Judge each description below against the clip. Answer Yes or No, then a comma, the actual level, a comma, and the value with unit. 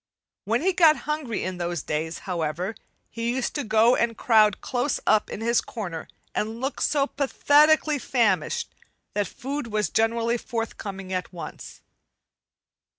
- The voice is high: Yes, high, 230 Hz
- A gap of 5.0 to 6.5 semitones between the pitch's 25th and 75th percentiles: Yes, wide, 5.6 semitones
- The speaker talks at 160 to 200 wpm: No, average, 145 wpm